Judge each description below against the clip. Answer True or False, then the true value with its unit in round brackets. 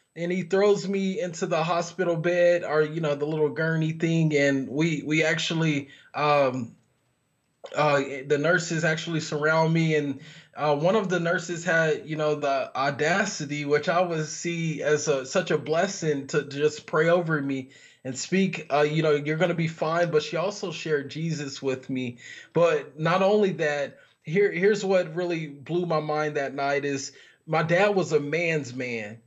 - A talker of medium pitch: True (155 Hz)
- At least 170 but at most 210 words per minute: True (180 wpm)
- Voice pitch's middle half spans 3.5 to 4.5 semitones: False (3.0 semitones)